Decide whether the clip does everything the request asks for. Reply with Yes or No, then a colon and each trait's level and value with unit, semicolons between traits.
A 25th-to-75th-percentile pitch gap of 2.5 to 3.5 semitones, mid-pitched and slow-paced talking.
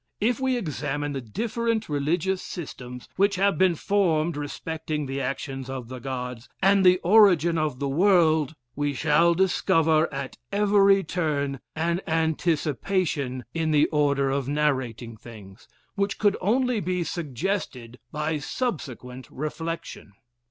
No: wide, 5.4 semitones; medium, 155 Hz; slow, 130 wpm